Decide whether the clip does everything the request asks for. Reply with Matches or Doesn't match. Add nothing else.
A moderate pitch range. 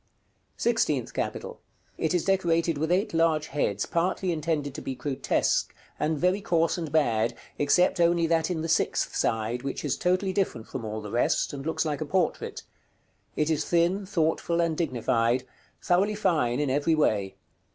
Matches